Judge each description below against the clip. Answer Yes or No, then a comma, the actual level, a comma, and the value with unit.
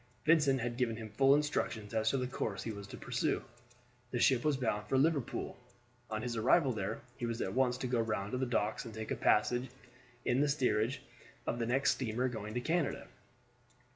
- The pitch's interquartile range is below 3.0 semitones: No, average, 3.3 semitones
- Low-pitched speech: Yes, low, 120 Hz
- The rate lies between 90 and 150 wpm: No, average, 200 wpm